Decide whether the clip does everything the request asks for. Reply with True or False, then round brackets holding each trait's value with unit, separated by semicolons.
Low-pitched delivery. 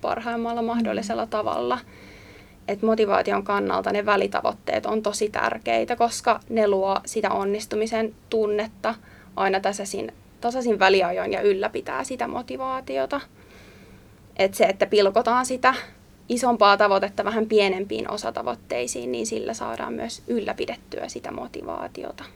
False (205 Hz)